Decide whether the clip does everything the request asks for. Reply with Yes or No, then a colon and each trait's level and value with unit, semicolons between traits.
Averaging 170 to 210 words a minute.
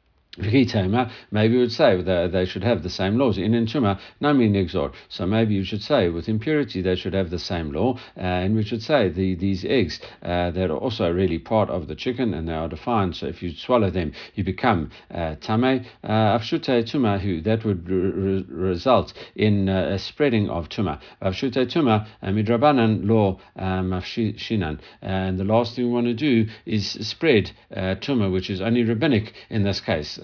Yes: average, 195 wpm